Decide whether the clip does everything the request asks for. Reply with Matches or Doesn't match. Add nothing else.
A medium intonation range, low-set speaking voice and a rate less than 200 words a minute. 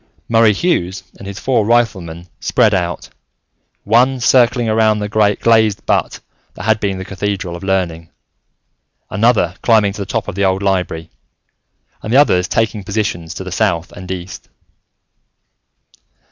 Matches